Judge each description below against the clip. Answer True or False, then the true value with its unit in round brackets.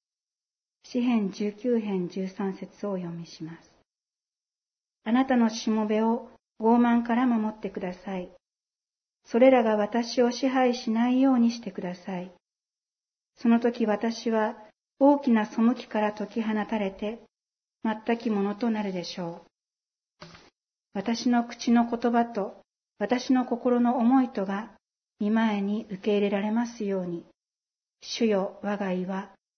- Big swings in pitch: False (3.1 semitones)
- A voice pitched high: True (220 Hz)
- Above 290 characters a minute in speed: False (240 characters per minute)